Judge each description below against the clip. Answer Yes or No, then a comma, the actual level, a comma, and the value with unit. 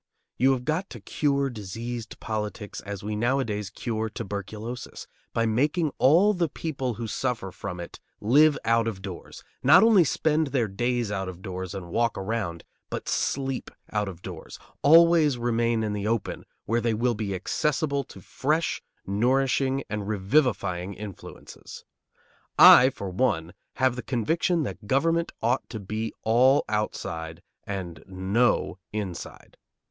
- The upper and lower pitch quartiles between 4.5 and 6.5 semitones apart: Yes, average, 5.2 semitones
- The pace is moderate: Yes, average, 145 wpm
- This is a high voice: No, low, 115 Hz